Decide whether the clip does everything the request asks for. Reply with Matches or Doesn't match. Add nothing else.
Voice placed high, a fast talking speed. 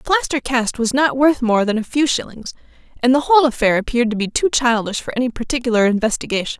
Matches